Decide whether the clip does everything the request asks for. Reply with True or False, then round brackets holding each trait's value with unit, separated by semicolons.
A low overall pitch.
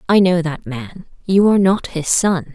False (180 Hz)